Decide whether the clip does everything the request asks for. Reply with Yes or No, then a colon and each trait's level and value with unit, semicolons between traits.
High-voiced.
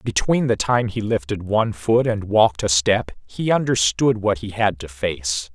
No: low, 105 Hz